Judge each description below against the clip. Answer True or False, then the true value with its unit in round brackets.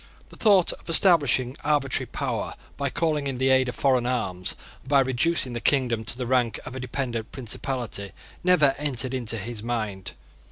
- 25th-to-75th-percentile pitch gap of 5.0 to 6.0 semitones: False (2.9 semitones)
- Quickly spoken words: False (175 wpm)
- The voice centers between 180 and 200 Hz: False (130 Hz)